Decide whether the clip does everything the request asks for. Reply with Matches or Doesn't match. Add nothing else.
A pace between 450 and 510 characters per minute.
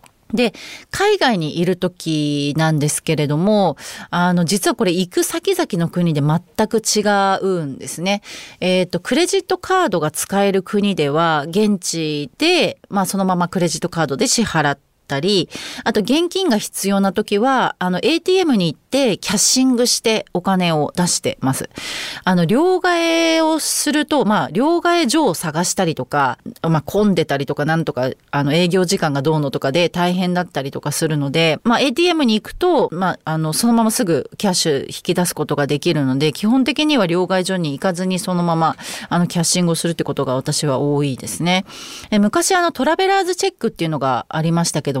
Doesn't match